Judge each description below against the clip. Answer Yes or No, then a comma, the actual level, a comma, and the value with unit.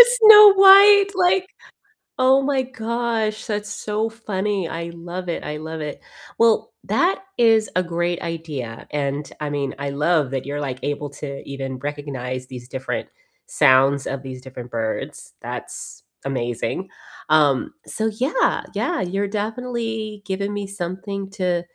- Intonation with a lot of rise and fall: Yes, wide, 7.8 semitones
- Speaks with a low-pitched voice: No, medium, 175 Hz